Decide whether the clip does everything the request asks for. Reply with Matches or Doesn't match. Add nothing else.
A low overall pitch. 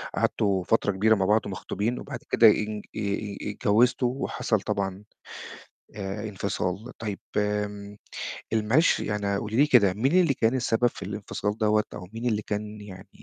Matches